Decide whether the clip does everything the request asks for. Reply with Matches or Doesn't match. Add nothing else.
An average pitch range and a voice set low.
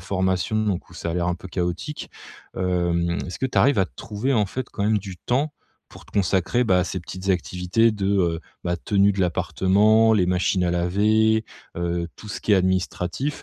Matches